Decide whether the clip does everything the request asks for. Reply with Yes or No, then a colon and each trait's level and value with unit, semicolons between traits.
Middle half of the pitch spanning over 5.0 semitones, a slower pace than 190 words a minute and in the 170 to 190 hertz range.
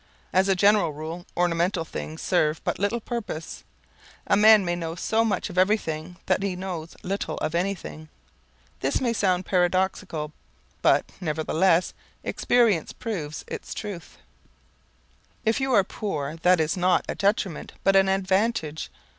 No: average, 3.6 semitones; average, 145 wpm; medium, 185 Hz